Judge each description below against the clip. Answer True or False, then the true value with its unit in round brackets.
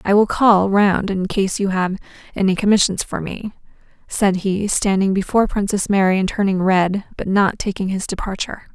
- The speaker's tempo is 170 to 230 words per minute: True (180 wpm)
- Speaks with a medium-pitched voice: False (195 Hz)